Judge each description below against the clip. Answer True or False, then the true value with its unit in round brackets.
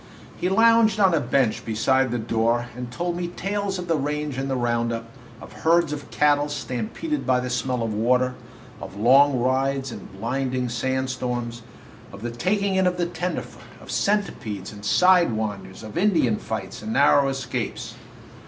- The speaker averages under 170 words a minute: False (175 wpm)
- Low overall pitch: True (130 Hz)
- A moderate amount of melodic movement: False (6.4 semitones)